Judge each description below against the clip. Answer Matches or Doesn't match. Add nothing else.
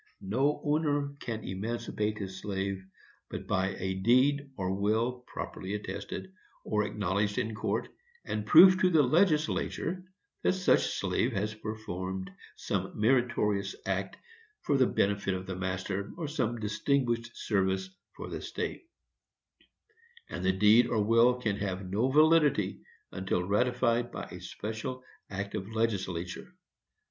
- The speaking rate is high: Doesn't match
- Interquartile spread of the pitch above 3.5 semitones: Matches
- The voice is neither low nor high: Doesn't match